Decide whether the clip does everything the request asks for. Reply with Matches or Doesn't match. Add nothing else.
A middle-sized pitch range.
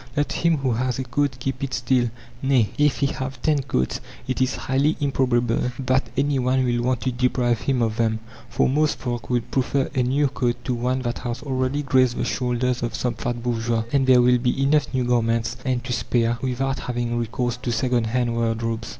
Doesn't match